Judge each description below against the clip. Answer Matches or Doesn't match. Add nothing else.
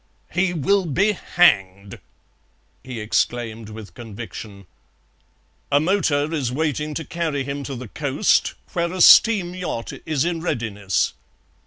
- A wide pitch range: Matches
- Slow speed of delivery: Matches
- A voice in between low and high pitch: Matches